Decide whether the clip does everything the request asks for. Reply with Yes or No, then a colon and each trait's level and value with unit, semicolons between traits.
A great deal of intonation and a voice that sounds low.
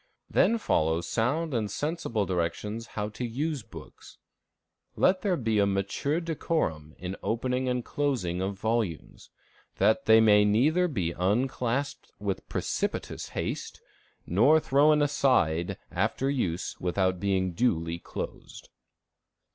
Yes: wide, 6.9 semitones; low, 110 Hz